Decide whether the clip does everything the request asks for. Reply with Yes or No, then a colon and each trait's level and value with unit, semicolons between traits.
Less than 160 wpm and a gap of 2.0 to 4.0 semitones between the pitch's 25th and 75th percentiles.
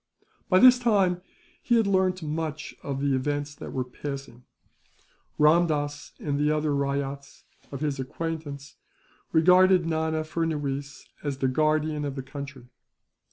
Yes: slow, 135 wpm; average, 2.8 semitones